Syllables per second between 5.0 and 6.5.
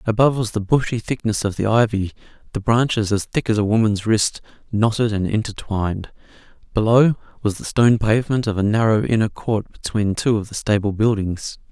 Yes: 5.5 syllables/s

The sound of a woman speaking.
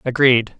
No: male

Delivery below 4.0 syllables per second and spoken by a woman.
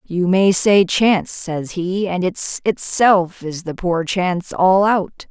Yes: 3.5 syllables/s; female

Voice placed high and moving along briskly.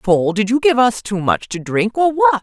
Yes: high, 215 Hz; fast, 275 wpm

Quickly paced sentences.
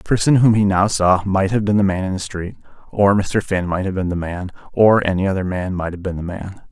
Yes: fast, 275 wpm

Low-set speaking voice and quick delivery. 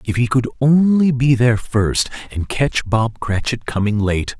No: low, 120 Hz; average, 180 wpm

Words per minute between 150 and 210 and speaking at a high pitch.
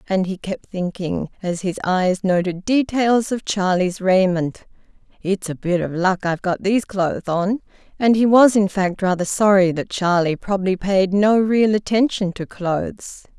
Yes: average, 170 wpm; high, 195 Hz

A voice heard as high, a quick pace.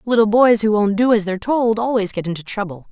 Yes: high, 215 Hz; fast, 245 wpm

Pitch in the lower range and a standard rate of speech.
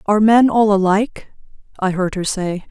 No: high, 205 Hz; average, 180 wpm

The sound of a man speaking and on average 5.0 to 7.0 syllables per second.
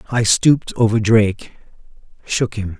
No: male; 4.8 syllables/s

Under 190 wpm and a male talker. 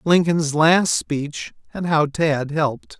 Yes: average, 140 wpm; male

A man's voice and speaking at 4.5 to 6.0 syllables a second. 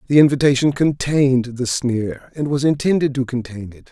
Yes: male; 5.2 syllables/s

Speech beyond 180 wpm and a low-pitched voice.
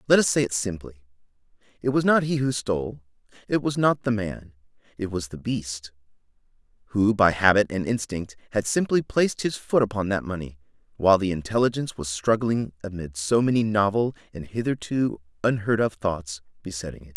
No: average, 170 wpm; low, 105 Hz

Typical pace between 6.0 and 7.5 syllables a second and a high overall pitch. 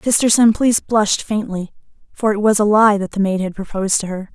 Yes: 6.1 syllables/s; high, 210 Hz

